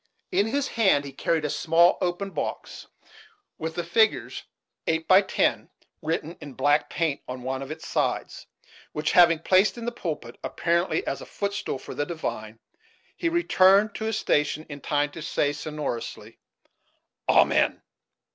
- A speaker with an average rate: Yes, average, 155 wpm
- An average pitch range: Yes, average, 4.9 semitones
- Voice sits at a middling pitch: Yes, medium, 165 Hz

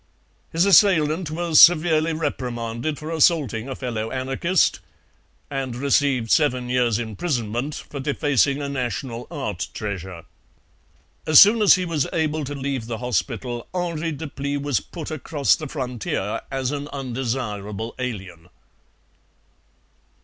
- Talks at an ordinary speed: No, slow, 125 wpm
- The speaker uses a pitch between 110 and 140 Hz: Yes, low, 135 Hz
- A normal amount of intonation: Yes, average, 4.5 semitones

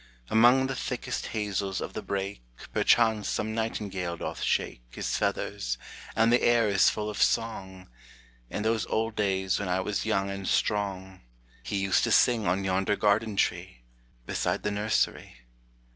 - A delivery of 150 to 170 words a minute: Yes, average, 160 wpm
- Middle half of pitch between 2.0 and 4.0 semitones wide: Yes, average, 2.7 semitones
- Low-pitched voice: Yes, low, 100 Hz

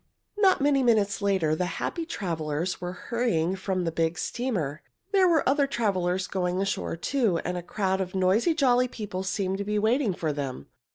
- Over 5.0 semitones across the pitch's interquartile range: Yes, wide, 5.4 semitones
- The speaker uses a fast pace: No, average, 180 wpm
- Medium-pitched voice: No, high, 195 Hz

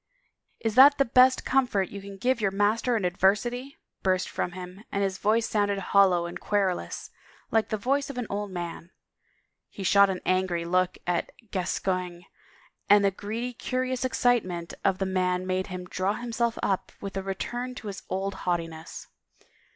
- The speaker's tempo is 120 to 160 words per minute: No, average, 175 wpm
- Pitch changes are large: No, average, 3.9 semitones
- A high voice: Yes, high, 195 Hz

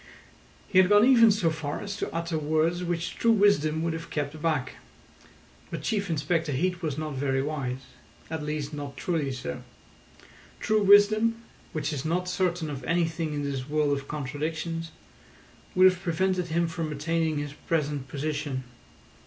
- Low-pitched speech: No, medium, 160 Hz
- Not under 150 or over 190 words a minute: Yes, average, 160 wpm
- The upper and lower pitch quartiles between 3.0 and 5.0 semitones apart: Yes, average, 3.4 semitones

